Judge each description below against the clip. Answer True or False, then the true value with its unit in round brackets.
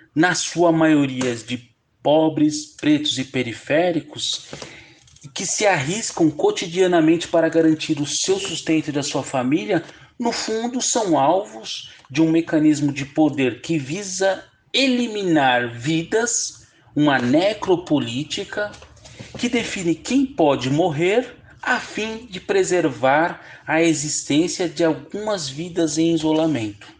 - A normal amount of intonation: True (5.0 semitones)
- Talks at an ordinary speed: False (115 wpm)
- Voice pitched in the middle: True (160 Hz)